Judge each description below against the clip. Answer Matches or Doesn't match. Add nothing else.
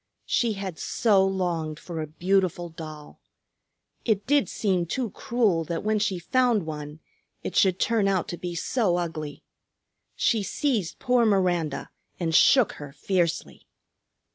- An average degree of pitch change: Matches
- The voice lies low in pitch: Doesn't match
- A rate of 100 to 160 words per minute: Matches